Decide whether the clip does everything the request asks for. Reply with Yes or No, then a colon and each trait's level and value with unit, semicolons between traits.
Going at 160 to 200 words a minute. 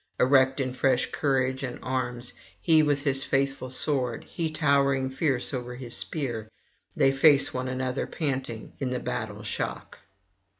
No: average, 145 wpm